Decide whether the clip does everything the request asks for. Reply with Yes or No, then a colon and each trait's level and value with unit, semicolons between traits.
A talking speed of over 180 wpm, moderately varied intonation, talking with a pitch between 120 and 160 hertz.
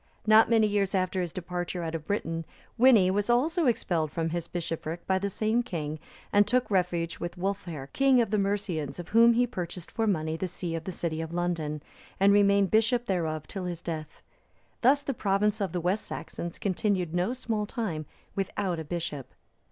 No: average, 190 wpm; average, 4.2 semitones; medium, 185 Hz